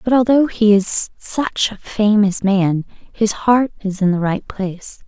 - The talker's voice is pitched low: No, high, 210 Hz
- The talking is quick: No, average, 180 wpm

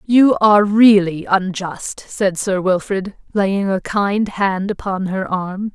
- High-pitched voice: Yes, high, 195 Hz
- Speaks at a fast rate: No, average, 145 wpm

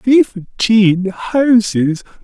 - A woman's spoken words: No, male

